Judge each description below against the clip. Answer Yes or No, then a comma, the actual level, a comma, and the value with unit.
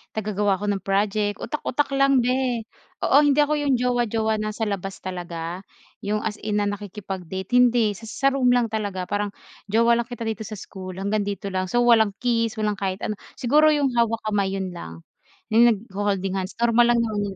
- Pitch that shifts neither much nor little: Yes, average, 3.4 semitones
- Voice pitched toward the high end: Yes, high, 215 Hz